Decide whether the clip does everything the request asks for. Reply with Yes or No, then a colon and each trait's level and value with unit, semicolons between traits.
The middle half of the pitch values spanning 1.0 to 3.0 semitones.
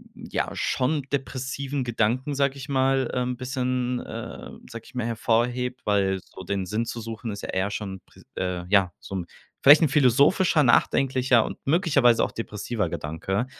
No: average, 4.2 semitones